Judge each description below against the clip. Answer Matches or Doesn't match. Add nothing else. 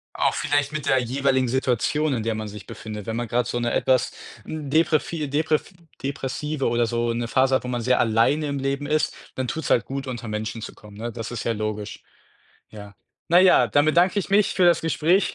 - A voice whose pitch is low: Matches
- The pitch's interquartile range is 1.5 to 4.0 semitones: Doesn't match